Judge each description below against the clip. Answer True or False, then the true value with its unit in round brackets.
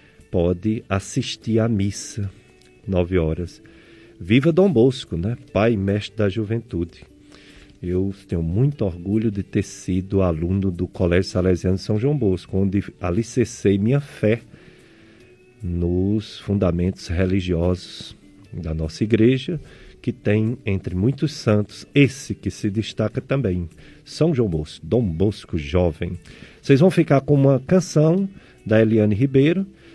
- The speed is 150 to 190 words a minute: False (130 wpm)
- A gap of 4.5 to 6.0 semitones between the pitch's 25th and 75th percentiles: True (4.8 semitones)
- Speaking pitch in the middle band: False (105 Hz)